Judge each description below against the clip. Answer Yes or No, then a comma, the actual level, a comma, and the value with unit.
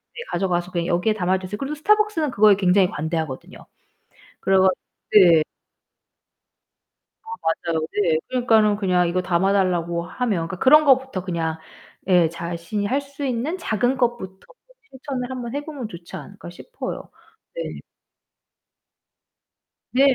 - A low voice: No, high, 200 Hz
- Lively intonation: Yes, wide, 6.7 semitones